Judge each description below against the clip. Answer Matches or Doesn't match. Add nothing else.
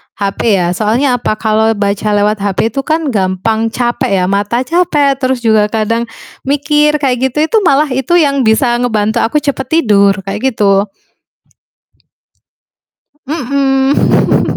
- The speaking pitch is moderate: Doesn't match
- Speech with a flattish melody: Doesn't match